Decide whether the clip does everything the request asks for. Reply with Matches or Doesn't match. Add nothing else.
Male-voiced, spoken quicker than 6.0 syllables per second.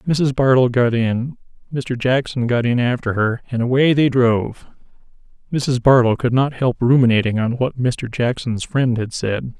Doesn't match